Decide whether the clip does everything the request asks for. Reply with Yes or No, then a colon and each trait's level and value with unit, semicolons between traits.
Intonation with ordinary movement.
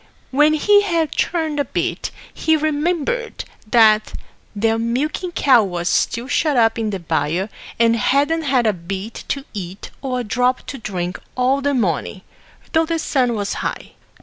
No: wide, 6.0 semitones